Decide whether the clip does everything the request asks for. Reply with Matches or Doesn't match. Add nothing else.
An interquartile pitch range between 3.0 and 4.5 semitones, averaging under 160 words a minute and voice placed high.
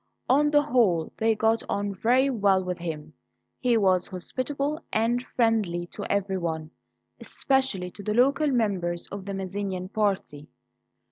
Doesn't match